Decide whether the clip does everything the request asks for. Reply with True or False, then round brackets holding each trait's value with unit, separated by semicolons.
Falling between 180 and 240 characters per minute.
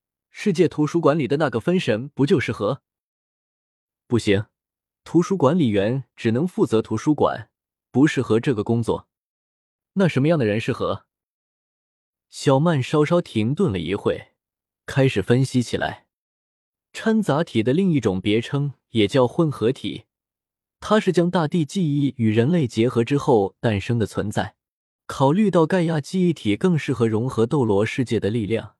True (235 characters per minute)